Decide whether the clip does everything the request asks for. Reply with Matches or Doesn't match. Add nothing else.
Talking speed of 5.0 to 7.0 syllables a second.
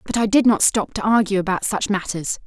Matches